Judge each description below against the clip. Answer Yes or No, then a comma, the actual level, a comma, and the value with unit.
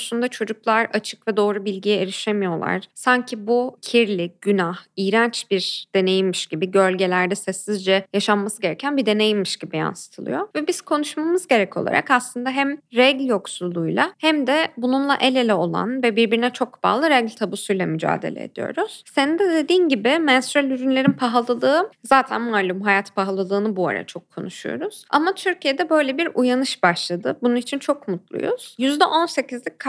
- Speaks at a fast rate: Yes, fast, 145 wpm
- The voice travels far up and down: Yes, wide, 5.9 semitones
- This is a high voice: Yes, high, 240 Hz